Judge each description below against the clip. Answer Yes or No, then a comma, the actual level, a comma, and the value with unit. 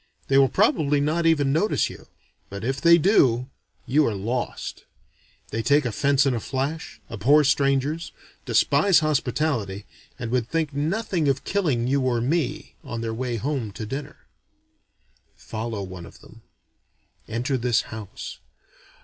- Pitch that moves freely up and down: No, average, 4.5 semitones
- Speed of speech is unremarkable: Yes, average, 145 wpm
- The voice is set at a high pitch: No, low, 135 Hz